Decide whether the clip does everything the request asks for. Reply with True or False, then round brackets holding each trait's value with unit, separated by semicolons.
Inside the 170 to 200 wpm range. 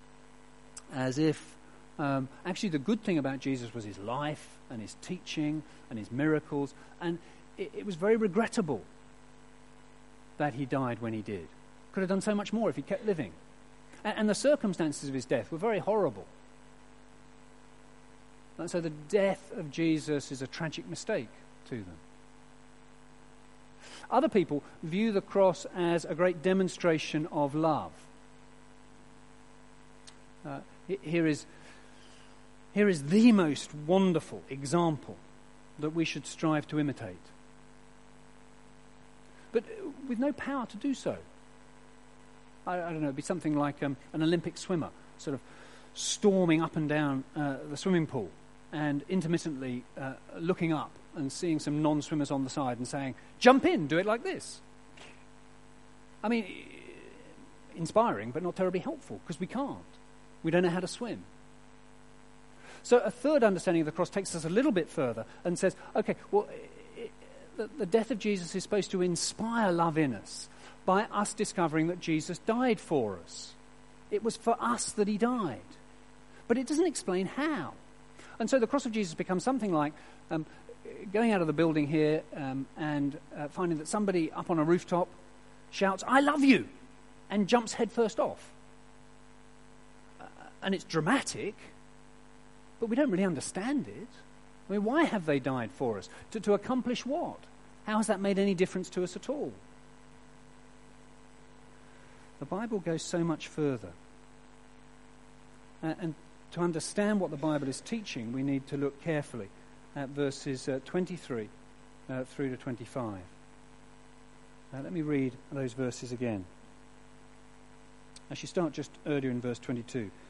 False (155 wpm)